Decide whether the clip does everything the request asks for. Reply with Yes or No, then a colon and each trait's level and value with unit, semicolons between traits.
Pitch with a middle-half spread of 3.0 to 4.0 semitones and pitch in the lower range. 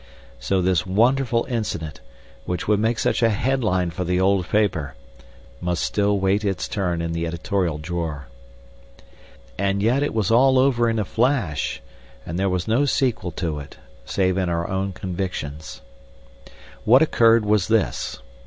No: average, 4.6 semitones; very low, 95 Hz